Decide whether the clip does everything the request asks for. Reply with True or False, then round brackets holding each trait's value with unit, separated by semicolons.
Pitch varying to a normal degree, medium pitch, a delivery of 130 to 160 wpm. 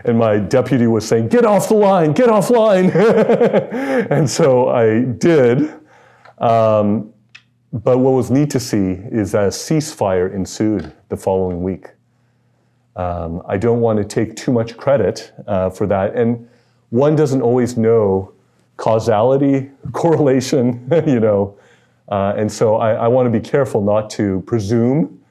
False (4.6 semitones; 120 Hz; 150 wpm)